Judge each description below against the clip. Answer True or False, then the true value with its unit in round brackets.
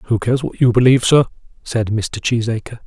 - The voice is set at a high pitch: False (115 Hz)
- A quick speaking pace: False (190 wpm)